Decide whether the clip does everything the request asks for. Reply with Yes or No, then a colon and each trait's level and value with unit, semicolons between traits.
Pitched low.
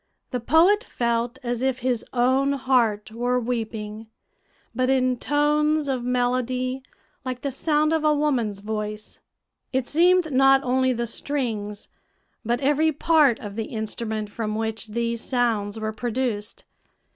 No: very high, 250 Hz